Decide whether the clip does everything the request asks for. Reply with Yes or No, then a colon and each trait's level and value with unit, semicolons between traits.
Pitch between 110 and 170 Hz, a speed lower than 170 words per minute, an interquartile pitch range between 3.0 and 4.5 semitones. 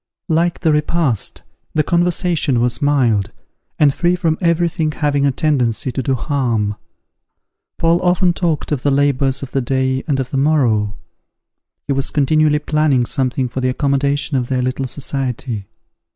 Yes: medium, 140 Hz; average, 160 wpm; average, 3.3 semitones